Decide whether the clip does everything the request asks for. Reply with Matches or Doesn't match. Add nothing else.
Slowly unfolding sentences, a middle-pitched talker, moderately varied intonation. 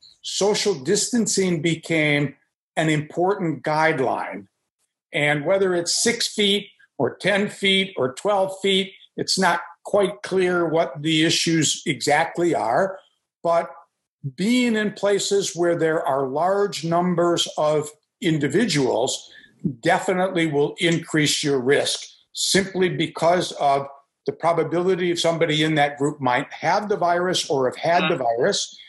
Matches